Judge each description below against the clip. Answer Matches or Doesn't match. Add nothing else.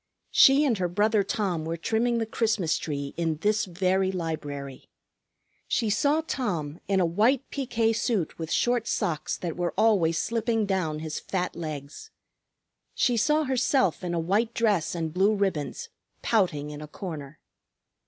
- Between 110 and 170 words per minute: Matches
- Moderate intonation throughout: Doesn't match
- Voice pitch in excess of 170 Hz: Matches